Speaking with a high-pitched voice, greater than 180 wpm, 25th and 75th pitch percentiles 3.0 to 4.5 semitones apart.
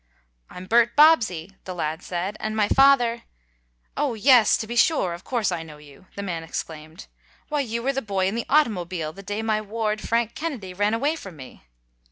No: high, 215 Hz; fast, 205 wpm; average, 4.9 semitones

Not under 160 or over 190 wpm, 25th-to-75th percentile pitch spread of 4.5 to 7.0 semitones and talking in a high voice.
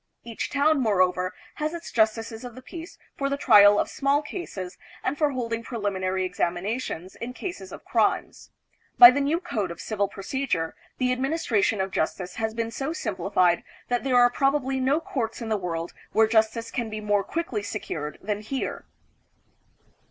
Yes: average, 170 wpm; average, 5.3 semitones; high, 225 Hz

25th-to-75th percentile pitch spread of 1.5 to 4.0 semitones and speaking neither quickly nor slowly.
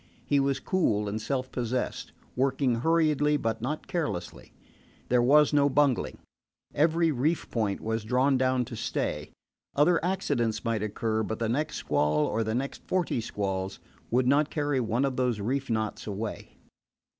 No: average, 4.6 semitones; average, 155 wpm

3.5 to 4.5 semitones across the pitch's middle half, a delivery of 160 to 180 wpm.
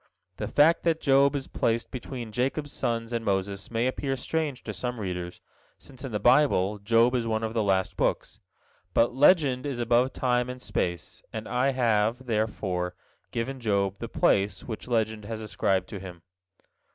Yes: average, 3.8 semitones; average, 175 wpm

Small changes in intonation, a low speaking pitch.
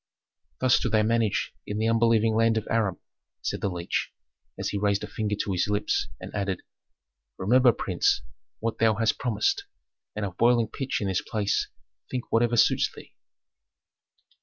Yes: narrow, 2.1 semitones; low, 110 Hz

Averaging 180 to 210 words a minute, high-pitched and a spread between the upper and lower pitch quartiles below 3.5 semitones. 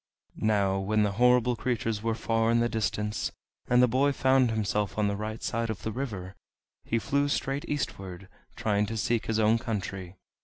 No: average, 185 wpm; low, 110 Hz; average, 2.9 semitones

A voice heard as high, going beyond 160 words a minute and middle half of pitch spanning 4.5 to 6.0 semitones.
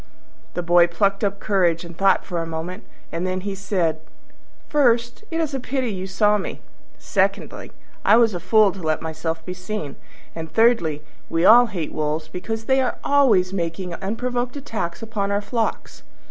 Yes: high, 195 Hz; average, 175 wpm; average, 4.9 semitones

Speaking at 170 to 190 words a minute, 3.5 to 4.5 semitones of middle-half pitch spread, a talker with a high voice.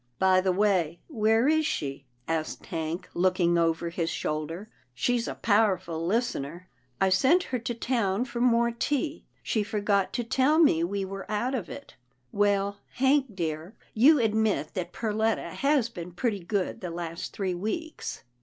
No: average, 180 wpm; wide, 5.5 semitones; high, 200 Hz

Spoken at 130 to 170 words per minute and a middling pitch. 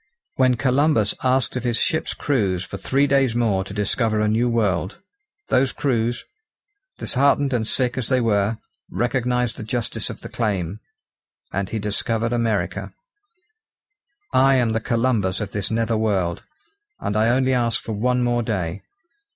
No: average, 155 wpm; low, 115 Hz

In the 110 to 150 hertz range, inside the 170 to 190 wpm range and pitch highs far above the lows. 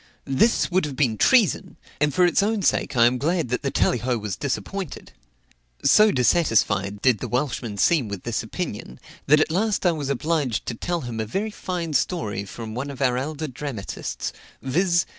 Yes: medium, 140 Hz; average, 185 wpm; wide, 6.5 semitones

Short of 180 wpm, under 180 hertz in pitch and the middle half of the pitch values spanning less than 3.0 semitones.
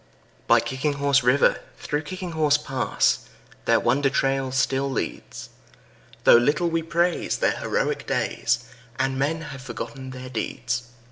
Yes: average, 140 wpm; medium, 140 Hz; narrow, 2.5 semitones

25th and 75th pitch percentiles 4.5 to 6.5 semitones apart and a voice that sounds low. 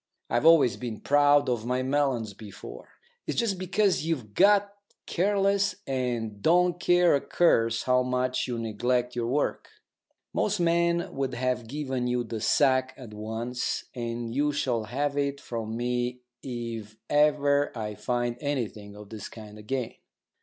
No: average, 3.9 semitones; low, 125 Hz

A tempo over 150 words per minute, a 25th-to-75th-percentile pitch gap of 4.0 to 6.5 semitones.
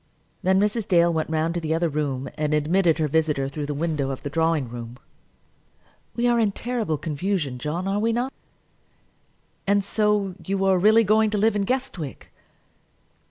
Yes: average, 175 wpm; wide, 5.4 semitones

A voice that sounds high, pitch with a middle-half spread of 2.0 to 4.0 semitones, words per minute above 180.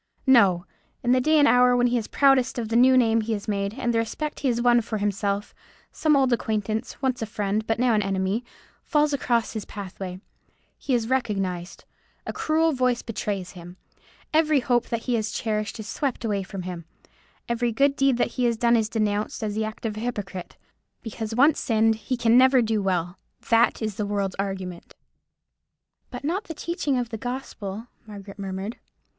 Yes: high, 225 Hz; average, 3.5 semitones; average, 195 wpm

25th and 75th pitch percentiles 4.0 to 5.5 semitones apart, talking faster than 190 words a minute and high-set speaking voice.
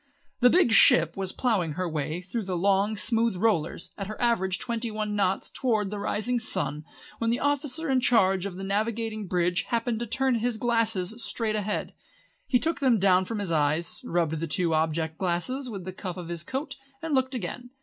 Yes: average, 4.8 semitones; average, 200 wpm; high, 205 Hz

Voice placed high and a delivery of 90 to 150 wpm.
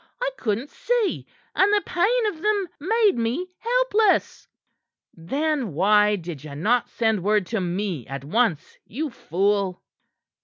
Yes: high, 230 Hz; average, 140 wpm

